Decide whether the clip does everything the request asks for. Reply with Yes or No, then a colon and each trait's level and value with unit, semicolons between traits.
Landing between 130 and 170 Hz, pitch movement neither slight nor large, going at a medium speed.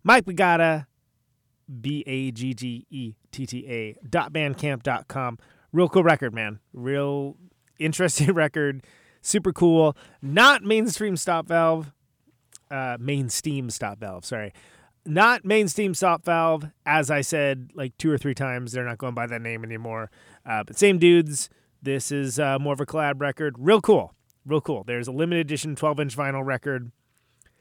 Yes: medium, 140 Hz; average, 4.4 semitones; average, 165 wpm